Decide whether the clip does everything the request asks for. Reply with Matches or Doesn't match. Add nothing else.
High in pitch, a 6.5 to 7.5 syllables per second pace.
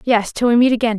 Matches